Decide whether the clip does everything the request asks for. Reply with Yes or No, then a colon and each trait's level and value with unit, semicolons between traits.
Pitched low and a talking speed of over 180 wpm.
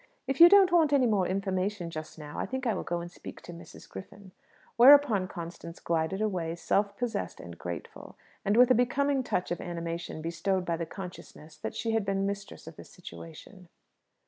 No: high, 190 Hz; average, 195 wpm